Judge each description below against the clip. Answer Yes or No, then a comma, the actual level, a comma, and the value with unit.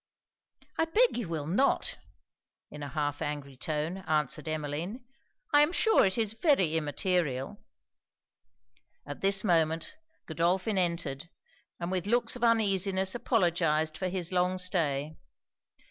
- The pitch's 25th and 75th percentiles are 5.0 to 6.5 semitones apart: No, average, 4.5 semitones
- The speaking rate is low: Yes, slow, 130 wpm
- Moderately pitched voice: Yes, medium, 175 Hz